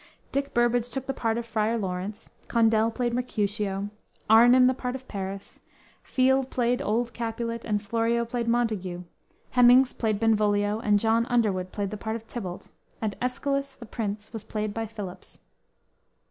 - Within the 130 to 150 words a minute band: No, average, 160 wpm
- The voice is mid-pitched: No, high, 225 Hz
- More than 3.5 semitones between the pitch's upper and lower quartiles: No, narrow, 2.6 semitones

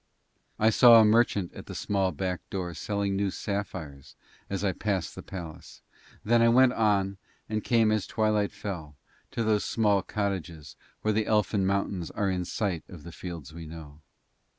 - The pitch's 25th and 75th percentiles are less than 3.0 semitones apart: No, average, 3.5 semitones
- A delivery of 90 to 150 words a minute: No, average, 175 wpm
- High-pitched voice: No, low, 100 Hz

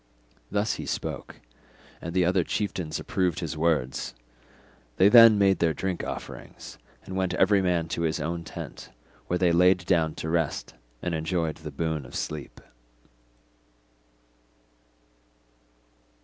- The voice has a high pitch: No, very low, 85 Hz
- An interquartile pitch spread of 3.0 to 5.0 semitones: No, narrow, 2.6 semitones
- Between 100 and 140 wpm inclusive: Yes, slow, 135 wpm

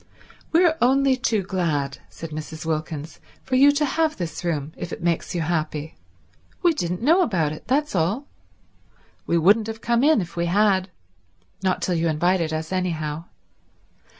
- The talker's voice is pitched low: No, medium, 175 Hz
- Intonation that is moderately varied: No, wide, 6.9 semitones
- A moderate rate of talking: Yes, average, 160 wpm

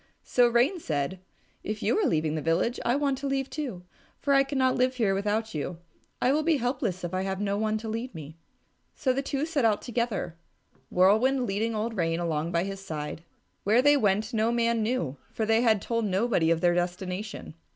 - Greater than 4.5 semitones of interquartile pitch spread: Yes, wide, 5.6 semitones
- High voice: Yes, high, 220 Hz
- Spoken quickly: Yes, fast, 210 wpm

